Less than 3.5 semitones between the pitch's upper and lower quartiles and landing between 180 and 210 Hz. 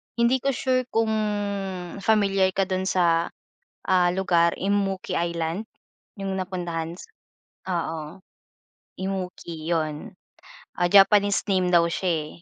Yes: narrow, 2.6 semitones; medium, 185 Hz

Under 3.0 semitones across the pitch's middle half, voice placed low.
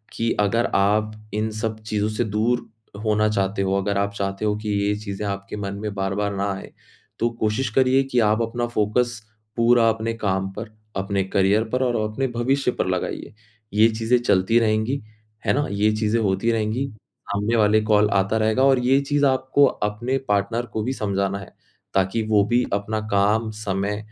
Yes: narrow, 2.6 semitones; low, 110 Hz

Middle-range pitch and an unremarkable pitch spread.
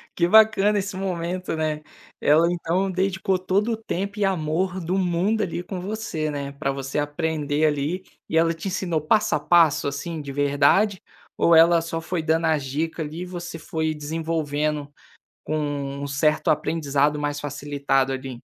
Yes: medium, 160 Hz; average, 3.9 semitones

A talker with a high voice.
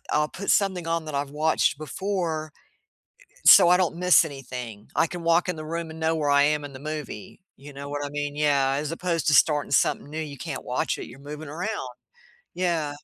No: medium, 155 Hz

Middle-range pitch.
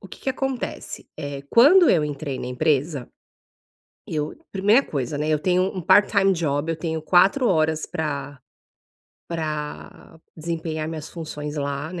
Yes: medium, 160 Hz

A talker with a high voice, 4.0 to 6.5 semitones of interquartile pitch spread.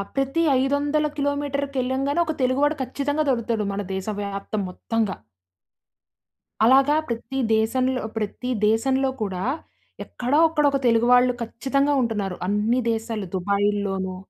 Yes: very high, 250 Hz; average, 4.6 semitones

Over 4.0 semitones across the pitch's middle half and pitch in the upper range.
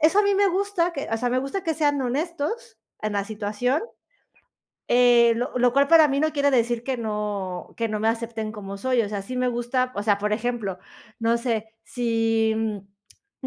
Yes: average, 4.4 semitones; high, 235 Hz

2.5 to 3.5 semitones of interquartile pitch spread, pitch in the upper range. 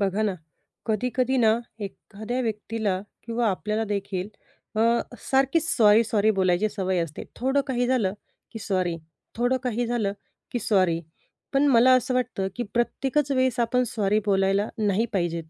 No: average, 4.0 semitones; high, 220 Hz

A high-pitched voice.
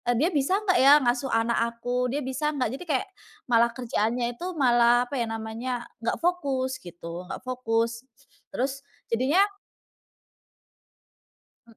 Yes: very high, 250 Hz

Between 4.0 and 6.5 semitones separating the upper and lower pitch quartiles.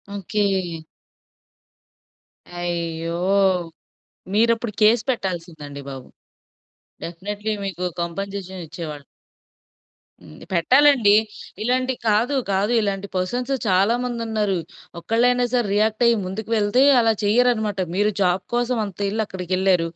Yes: average, 4.3 semitones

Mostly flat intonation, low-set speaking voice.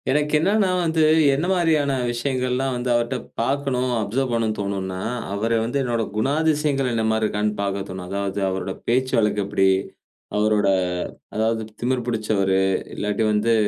No: average, 4.4 semitones; low, 115 Hz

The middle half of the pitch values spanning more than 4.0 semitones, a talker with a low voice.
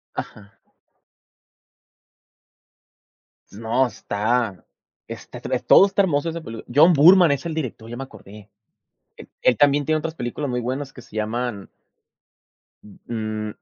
Yes: wide, 5.5 semitones; low, 125 Hz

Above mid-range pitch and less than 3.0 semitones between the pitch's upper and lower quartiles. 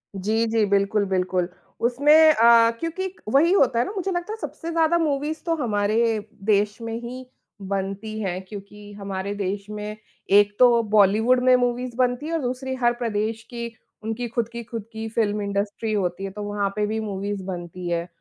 No: high, 220 Hz; average, 3.5 semitones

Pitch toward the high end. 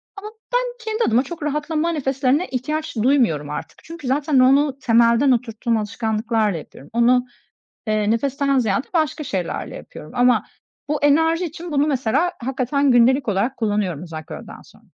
Yes: very high, 255 Hz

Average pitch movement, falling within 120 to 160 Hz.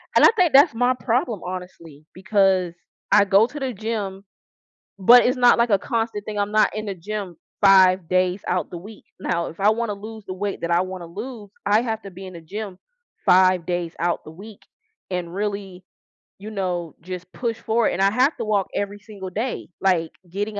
No: average, 3.1 semitones; high, 200 Hz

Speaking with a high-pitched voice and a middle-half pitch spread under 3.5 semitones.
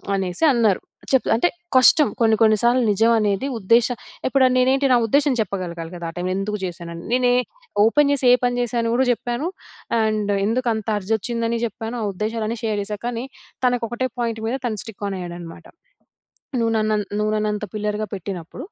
Yes: high, 225 Hz; average, 3.1 semitones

